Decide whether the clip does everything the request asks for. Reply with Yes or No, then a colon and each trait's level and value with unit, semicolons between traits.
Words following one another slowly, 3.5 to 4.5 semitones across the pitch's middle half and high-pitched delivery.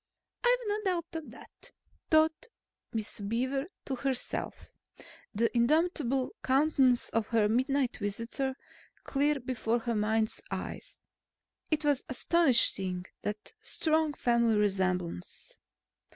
No: slow, 110 wpm; average, 5.2 semitones; very high, 255 Hz